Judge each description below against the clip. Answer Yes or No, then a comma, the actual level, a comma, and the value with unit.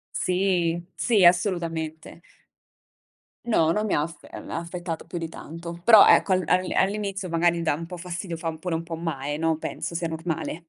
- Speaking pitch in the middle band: Yes, medium, 170 Hz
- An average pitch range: No, narrow, 2.0 semitones